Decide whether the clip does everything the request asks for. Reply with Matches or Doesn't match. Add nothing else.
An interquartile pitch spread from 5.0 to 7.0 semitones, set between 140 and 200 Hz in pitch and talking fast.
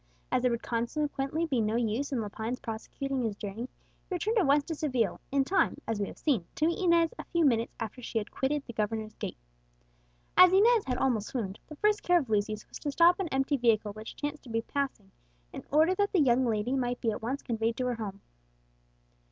Doesn't match